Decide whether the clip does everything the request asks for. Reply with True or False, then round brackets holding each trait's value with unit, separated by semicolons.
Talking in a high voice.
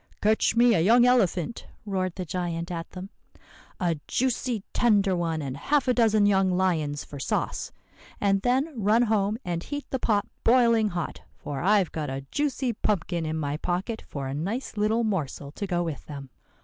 True (195 Hz)